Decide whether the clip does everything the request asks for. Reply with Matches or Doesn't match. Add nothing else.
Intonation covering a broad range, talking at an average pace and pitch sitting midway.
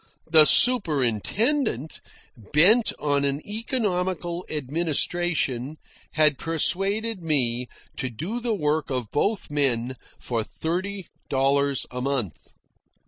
Doesn't match